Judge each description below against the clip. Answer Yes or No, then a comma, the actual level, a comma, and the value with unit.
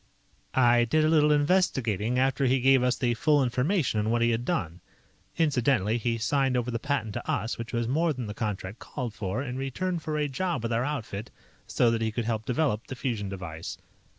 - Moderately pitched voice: No, low, 125 Hz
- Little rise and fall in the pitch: No, average, 3.7 semitones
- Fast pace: Yes, fast, 210 wpm